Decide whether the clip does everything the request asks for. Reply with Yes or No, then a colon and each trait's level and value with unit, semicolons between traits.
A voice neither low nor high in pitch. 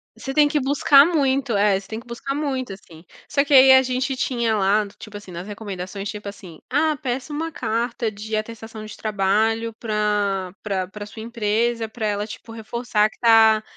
No: high, 225 Hz